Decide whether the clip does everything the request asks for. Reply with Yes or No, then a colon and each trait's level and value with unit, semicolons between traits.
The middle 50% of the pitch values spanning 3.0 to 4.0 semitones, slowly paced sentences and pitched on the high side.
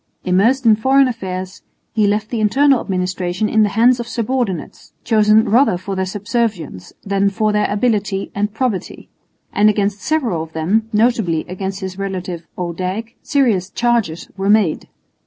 No: average, 3.5 semitones; average, 155 wpm; high, 205 Hz